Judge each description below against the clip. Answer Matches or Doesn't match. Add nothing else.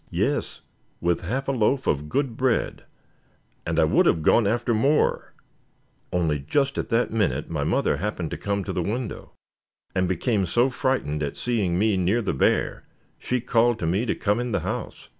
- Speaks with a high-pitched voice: Doesn't match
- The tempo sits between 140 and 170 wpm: Doesn't match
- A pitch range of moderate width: Doesn't match